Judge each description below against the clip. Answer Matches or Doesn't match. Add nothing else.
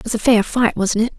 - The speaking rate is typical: Doesn't match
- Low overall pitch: Doesn't match